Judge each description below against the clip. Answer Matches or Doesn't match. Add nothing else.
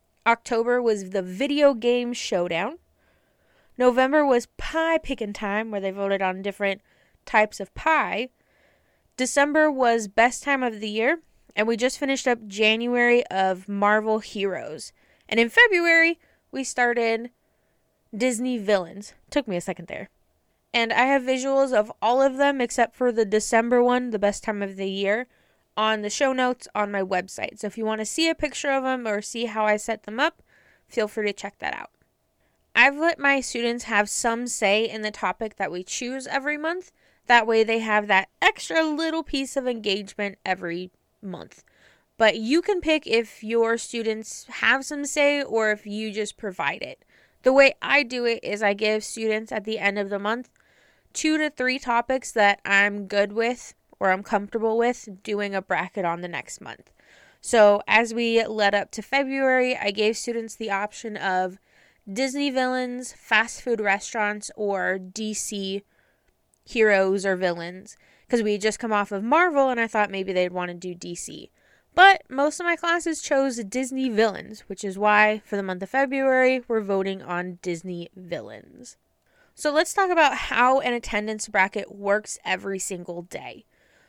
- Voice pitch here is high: Matches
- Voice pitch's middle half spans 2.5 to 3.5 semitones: Doesn't match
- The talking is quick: Doesn't match